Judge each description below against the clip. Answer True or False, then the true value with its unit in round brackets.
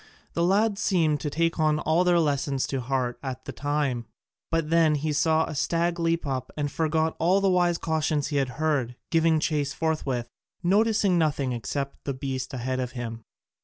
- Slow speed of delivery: False (180 wpm)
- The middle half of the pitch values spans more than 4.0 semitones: False (3.6 semitones)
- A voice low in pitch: False (150 Hz)